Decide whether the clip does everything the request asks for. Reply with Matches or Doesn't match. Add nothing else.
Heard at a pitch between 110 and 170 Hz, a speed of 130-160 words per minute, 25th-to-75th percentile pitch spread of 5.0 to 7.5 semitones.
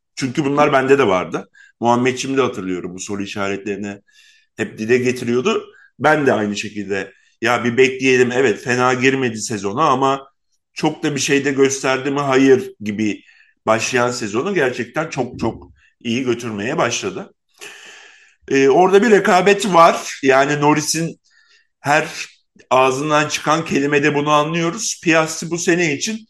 Matches